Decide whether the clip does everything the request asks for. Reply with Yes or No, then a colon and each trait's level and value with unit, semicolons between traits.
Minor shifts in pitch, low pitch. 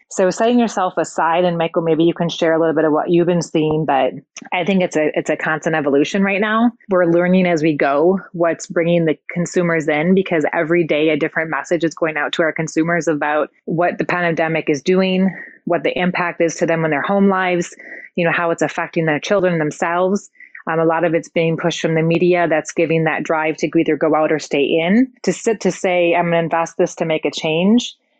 No: narrow, 2.1 semitones; medium, 170 Hz